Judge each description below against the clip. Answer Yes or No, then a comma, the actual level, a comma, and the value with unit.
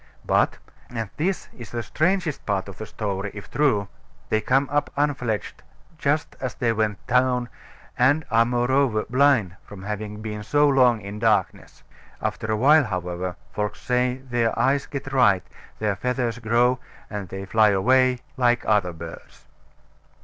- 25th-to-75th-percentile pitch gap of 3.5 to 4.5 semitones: Yes, average, 4.0 semitones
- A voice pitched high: No, low, 115 Hz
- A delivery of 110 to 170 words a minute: Yes, average, 155 wpm